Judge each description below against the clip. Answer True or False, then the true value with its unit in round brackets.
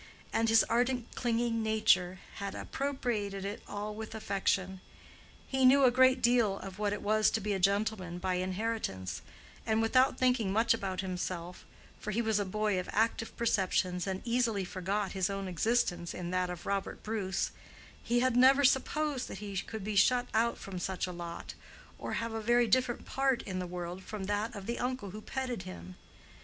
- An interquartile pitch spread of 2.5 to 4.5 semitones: True (3.9 semitones)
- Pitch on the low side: False (210 Hz)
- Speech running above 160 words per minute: True (180 wpm)